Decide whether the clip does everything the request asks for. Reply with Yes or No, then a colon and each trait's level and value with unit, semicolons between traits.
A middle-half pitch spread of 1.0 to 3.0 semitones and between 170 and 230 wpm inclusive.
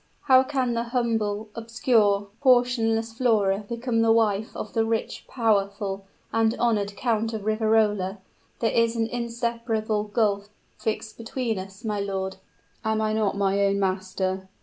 No: narrow, 2.4 semitones; average, 145 wpm